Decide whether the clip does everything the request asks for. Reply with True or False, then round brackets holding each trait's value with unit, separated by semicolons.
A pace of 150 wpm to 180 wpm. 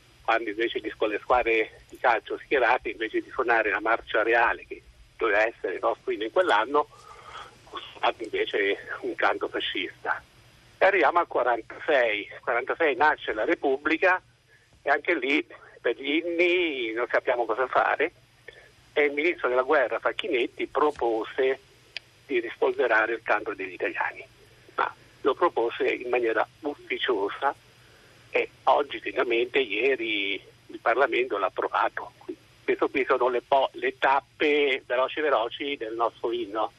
False (135 wpm)